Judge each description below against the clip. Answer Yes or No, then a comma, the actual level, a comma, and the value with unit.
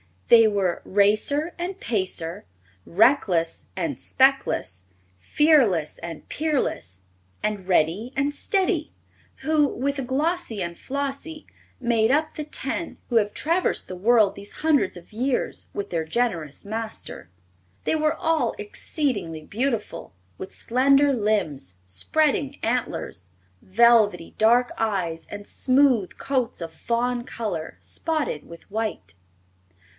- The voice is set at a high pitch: Yes, high, 230 Hz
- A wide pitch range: Yes, wide, 7.1 semitones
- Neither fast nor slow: No, slow, 120 wpm